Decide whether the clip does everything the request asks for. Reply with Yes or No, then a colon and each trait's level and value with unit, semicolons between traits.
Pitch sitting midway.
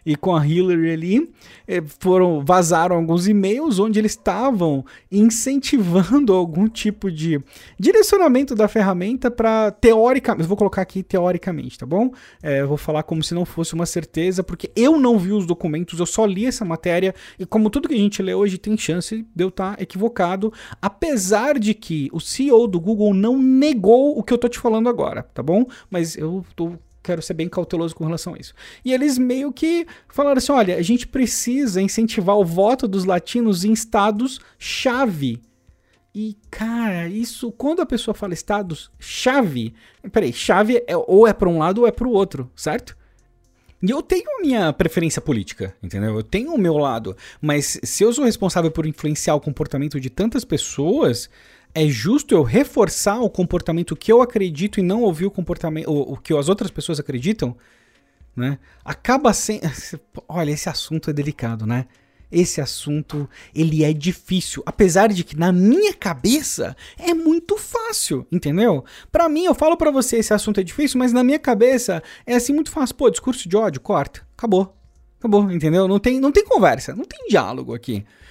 No: high, 195 Hz